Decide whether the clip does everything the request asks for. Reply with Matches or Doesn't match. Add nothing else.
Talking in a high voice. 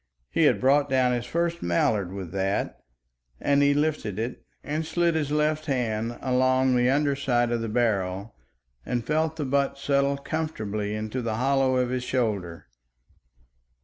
Doesn't match